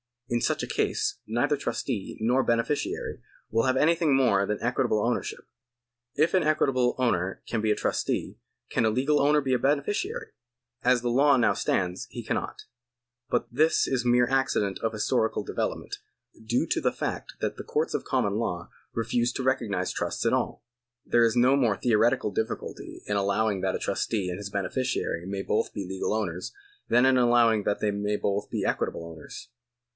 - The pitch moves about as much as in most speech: Yes, average, 4.1 semitones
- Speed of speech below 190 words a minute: Yes, average, 180 wpm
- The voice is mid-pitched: No, low, 115 Hz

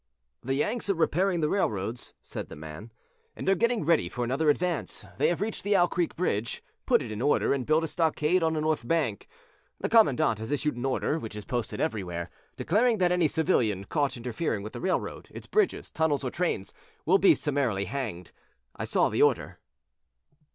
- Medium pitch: Yes, medium, 150 Hz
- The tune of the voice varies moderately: No, wide, 7.5 semitones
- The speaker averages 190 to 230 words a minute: Yes, average, 195 wpm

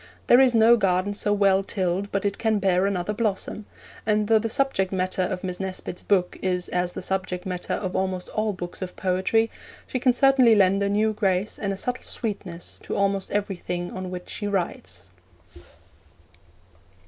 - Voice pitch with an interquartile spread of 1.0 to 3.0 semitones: Yes, narrow, 2.6 semitones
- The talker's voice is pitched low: No, high, 195 Hz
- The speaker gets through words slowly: No, average, 180 wpm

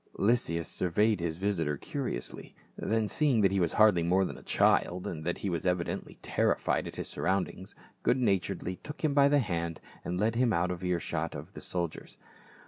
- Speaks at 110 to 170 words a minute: No, average, 195 wpm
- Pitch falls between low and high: No, very low, 95 Hz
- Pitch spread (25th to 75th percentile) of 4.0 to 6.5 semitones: Yes, average, 4.4 semitones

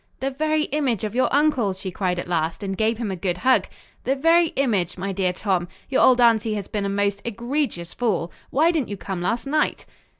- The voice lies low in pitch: No, high, 215 Hz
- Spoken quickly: Yes, fast, 220 wpm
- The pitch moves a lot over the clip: Yes, wide, 6.0 semitones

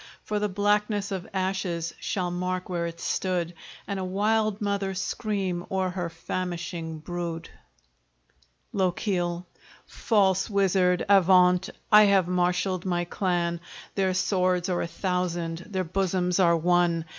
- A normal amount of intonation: No, narrow, 1.8 semitones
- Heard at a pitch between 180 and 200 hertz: Yes, medium, 185 Hz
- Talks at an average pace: No, slow, 130 wpm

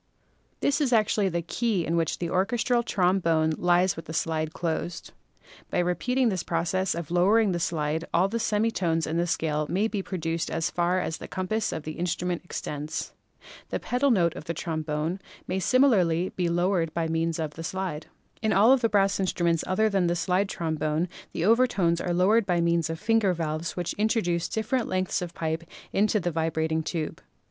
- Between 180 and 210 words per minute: Yes, average, 190 wpm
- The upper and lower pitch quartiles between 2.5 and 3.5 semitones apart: Yes, average, 3.2 semitones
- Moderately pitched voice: Yes, medium, 175 Hz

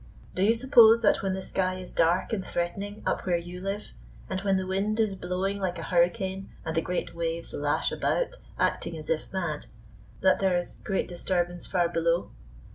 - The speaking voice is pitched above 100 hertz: Yes, medium, 185 Hz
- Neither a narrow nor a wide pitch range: No, narrow, 2.2 semitones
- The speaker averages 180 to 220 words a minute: Yes, average, 195 wpm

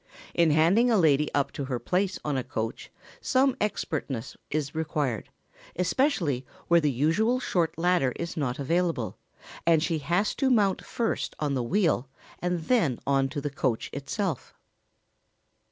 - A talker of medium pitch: Yes, medium, 160 Hz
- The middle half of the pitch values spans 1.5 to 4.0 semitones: No, average, 4.9 semitones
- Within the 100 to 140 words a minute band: No, average, 155 wpm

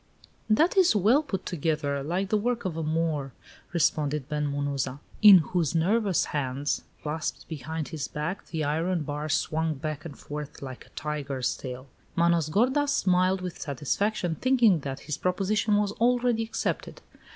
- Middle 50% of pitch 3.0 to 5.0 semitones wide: No, wide, 5.5 semitones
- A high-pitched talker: No, medium, 160 Hz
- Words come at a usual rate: Yes, average, 160 wpm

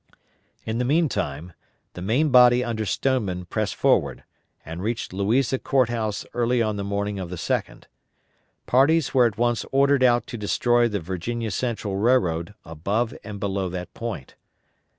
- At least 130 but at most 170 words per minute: Yes, average, 155 wpm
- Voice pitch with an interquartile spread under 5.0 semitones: Yes, average, 4.1 semitones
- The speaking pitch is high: No, low, 110 Hz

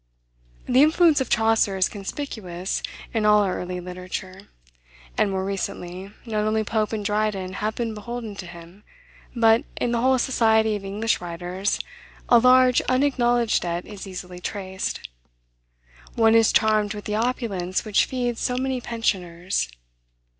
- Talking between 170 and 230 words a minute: No, average, 145 wpm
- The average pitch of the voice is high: Yes, high, 210 Hz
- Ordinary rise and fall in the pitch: Yes, average, 3.8 semitones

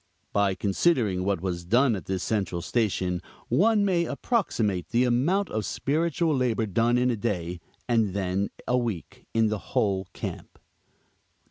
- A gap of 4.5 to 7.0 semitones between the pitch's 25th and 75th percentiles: Yes, average, 4.9 semitones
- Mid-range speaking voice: No, low, 110 Hz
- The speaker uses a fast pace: No, average, 155 wpm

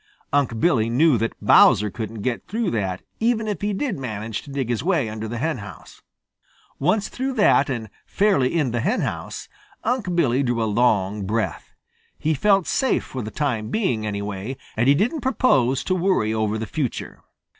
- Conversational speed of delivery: Yes, average, 175 wpm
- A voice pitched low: Yes, low, 130 Hz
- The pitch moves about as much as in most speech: No, wide, 9.0 semitones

